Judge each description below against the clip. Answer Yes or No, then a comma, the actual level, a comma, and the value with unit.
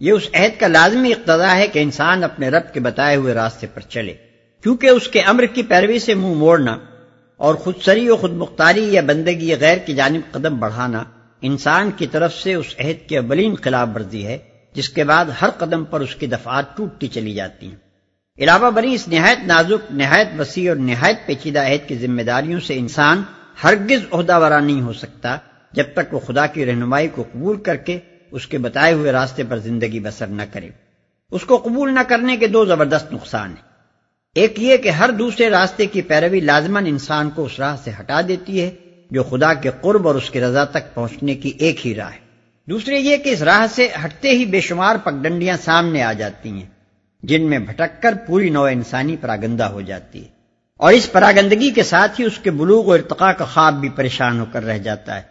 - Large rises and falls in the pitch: Yes, wide, 7.0 semitones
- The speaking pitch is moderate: Yes, medium, 155 Hz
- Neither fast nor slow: No, fast, 210 wpm